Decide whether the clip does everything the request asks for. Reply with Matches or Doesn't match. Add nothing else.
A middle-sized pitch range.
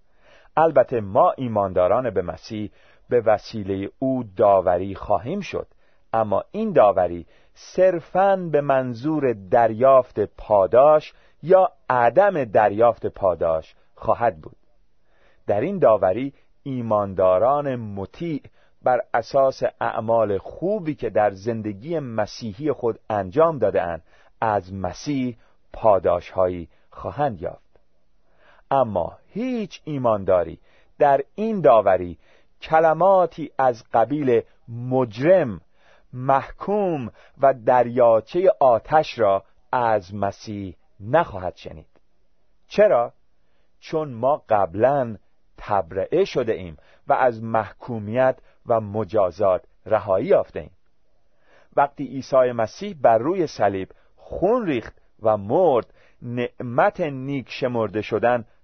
Doesn't match